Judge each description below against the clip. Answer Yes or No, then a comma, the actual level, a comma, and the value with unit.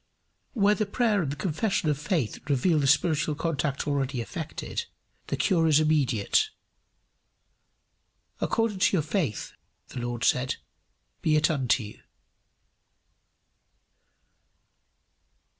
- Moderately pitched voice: Yes, medium, 155 Hz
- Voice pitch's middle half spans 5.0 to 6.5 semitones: Yes, wide, 5.4 semitones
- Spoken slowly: Yes, slow, 110 wpm